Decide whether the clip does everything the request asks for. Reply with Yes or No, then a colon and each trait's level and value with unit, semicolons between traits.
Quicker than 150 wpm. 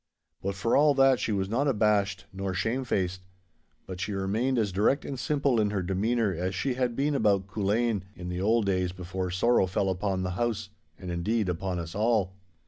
Yes: average, 200 wpm